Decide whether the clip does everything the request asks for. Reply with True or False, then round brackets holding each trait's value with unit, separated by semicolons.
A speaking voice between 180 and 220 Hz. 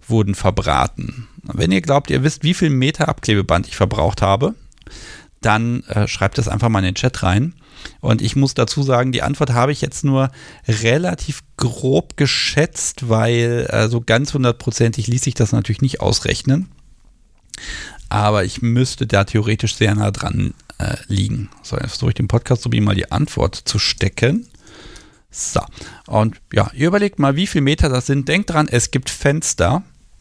False (120 Hz)